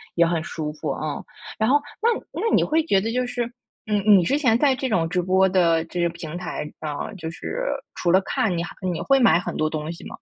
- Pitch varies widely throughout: Yes, wide, 5.8 semitones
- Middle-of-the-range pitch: Yes, medium, 180 Hz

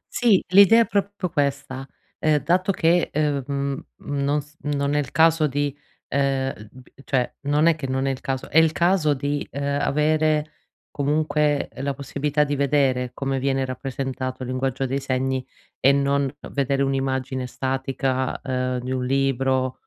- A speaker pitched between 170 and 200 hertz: No, medium, 140 Hz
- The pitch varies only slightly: Yes, narrow, 2.1 semitones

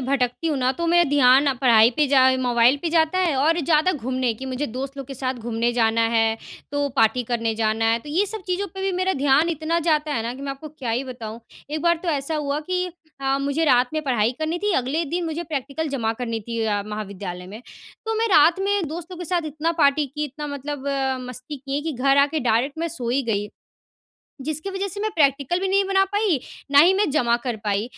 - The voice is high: Yes, very high, 280 Hz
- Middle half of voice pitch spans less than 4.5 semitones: No, average, 4.8 semitones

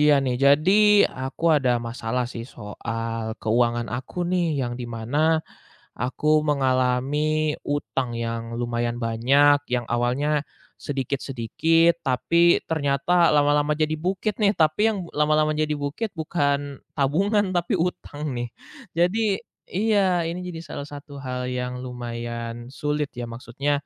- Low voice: No, medium, 145 Hz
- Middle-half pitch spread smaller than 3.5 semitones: No, average, 4.6 semitones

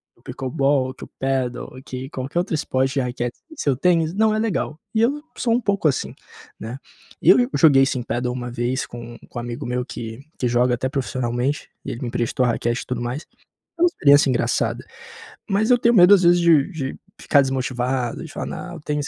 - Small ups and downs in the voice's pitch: No, wide, 5.6 semitones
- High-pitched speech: No, low, 135 Hz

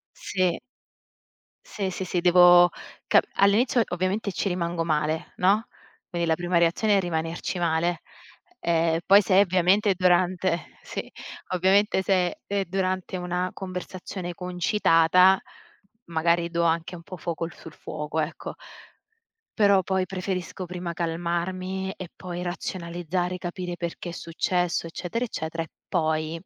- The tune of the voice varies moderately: No, narrow, 1.8 semitones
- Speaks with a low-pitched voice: No, medium, 180 Hz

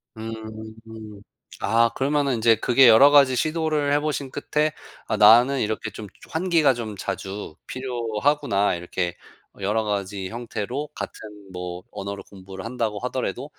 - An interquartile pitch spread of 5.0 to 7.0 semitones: Yes, wide, 5.4 semitones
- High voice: No, low, 115 Hz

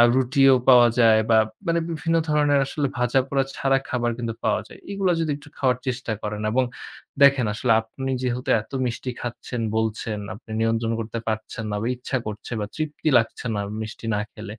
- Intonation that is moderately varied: Yes, average, 3.3 semitones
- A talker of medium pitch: No, low, 125 Hz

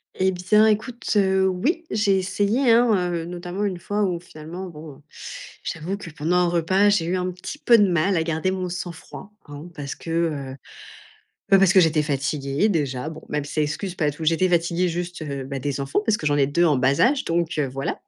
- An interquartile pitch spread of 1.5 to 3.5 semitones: No, average, 4.1 semitones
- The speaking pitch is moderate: Yes, medium, 175 Hz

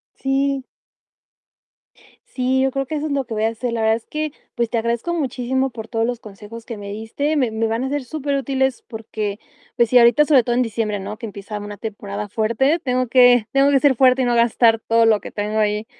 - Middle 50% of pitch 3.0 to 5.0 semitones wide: Yes, average, 3.3 semitones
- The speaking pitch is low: No, high, 235 Hz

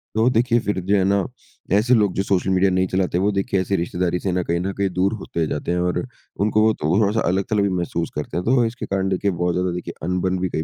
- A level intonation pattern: Yes, narrow, 2.2 semitones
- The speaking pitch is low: Yes, very low, 95 Hz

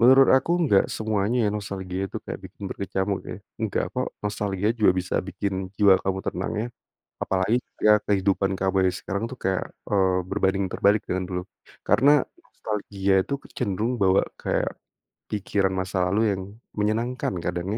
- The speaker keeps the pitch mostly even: Yes, narrow, 1.8 semitones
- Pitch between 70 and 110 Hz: Yes, low, 100 Hz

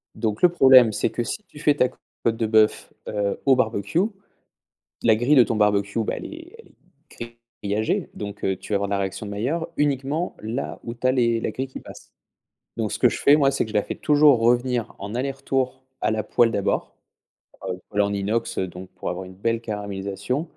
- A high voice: No, low, 115 Hz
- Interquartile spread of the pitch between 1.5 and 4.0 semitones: No, average, 4.5 semitones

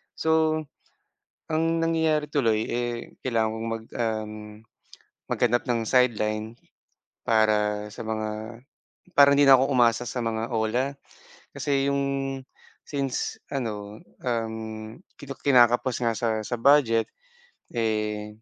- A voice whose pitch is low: Yes, low, 115 Hz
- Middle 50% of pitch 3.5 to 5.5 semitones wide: Yes, average, 3.8 semitones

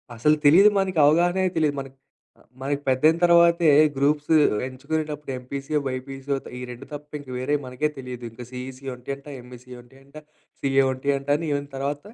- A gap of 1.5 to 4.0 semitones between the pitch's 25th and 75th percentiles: Yes, average, 2.7 semitones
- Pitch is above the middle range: No, medium, 140 Hz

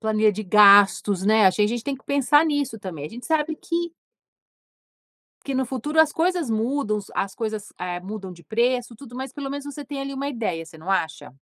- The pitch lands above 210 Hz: Yes, high, 230 Hz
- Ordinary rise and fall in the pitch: No, wide, 5.9 semitones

